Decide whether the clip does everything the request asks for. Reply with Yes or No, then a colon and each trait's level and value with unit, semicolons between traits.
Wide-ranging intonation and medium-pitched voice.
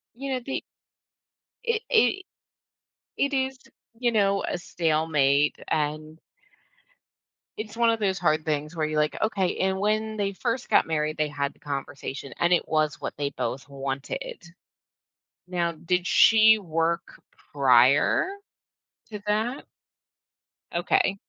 Yes: wide, 6.2 semitones; medium, 170 Hz